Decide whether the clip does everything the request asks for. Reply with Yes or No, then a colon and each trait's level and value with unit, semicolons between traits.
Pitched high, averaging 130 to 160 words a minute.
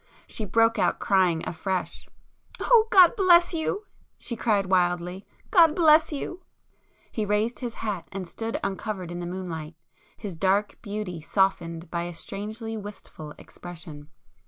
Yes: high, 200 Hz; slow, 135 wpm